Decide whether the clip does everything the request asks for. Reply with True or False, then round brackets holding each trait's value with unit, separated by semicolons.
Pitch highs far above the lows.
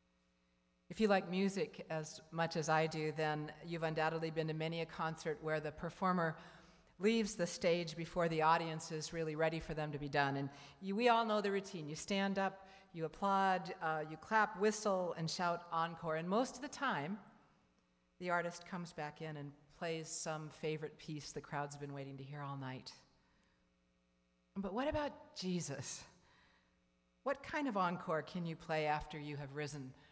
False (3.5 semitones)